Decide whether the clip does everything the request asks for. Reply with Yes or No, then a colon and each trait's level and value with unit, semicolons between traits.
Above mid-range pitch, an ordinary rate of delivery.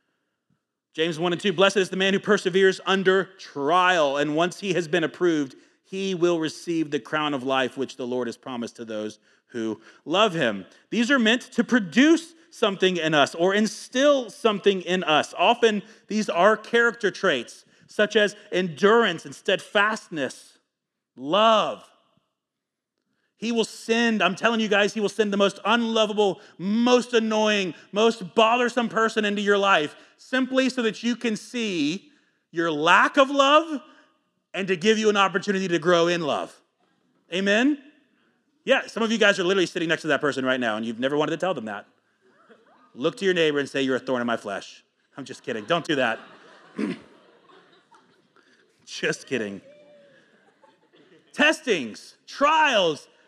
Yes: high, 200 Hz; average, 165 wpm